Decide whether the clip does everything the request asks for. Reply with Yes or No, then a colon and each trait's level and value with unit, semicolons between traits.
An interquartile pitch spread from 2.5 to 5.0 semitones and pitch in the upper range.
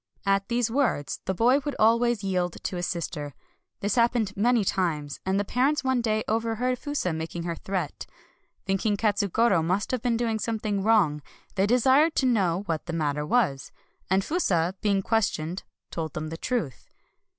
No: wide, 5.4 semitones; high, 205 Hz